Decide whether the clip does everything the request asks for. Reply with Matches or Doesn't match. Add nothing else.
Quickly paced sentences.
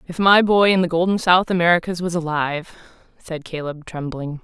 Doesn't match